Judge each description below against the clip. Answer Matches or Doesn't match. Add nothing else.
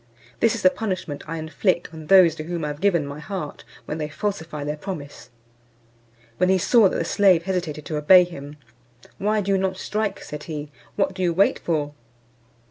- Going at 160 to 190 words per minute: Doesn't match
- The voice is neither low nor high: Matches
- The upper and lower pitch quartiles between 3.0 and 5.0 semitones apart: Matches